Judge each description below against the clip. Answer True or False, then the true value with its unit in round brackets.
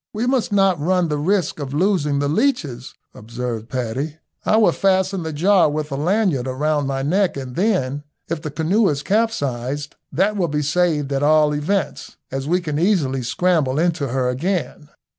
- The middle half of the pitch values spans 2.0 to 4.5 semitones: False (5.3 semitones)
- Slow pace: False (180 wpm)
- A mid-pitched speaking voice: True (155 Hz)